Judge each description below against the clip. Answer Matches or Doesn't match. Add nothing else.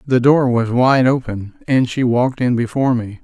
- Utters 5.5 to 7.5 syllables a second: Doesn't match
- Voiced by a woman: Doesn't match